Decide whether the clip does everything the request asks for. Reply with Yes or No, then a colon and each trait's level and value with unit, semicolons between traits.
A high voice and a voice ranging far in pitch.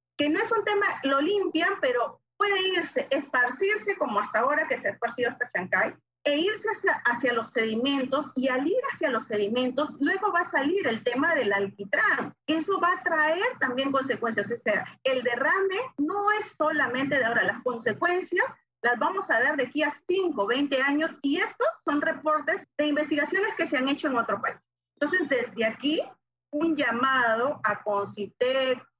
Yes: very high, 295 Hz; wide, 5.8 semitones